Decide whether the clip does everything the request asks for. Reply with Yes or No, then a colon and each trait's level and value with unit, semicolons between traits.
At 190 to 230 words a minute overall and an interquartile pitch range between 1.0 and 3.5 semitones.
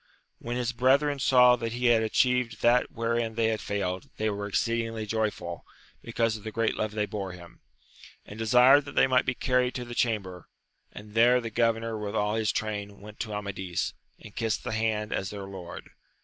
Yes: average, 195 wpm; narrow, 2.5 semitones